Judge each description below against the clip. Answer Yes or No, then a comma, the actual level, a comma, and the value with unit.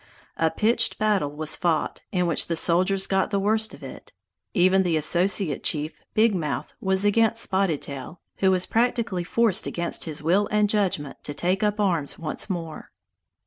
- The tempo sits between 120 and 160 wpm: No, average, 175 wpm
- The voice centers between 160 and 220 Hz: Yes, medium, 185 Hz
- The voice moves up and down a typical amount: Yes, average, 4.2 semitones